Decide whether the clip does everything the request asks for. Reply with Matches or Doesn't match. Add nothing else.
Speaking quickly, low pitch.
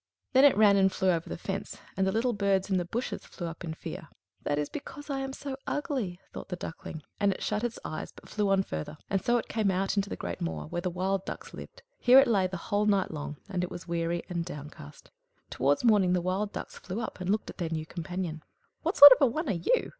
Doesn't match